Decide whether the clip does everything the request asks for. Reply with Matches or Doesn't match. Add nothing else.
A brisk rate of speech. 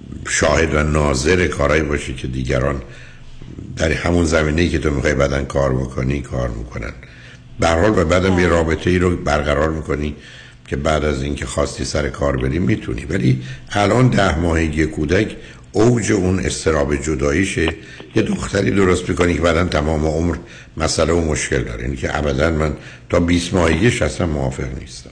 Matches